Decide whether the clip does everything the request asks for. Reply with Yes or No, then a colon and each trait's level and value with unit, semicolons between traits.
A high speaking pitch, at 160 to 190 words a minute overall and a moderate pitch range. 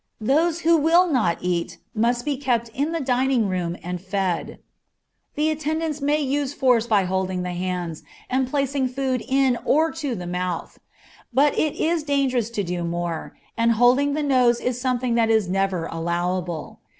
No: high, 245 Hz; average, 170 wpm; wide, 7.4 semitones